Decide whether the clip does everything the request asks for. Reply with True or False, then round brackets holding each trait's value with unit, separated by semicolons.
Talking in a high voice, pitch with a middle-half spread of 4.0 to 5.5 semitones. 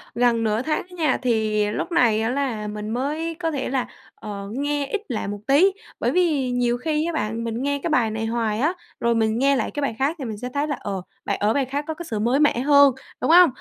True (255 Hz; 4.7 semitones)